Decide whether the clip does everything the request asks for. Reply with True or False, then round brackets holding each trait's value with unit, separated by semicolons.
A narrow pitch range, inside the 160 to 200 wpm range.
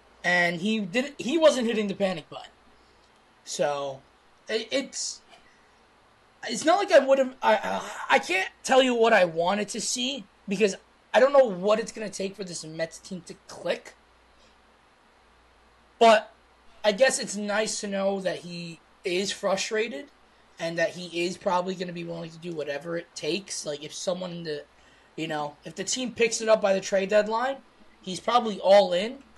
False (4.7 semitones; 180 wpm)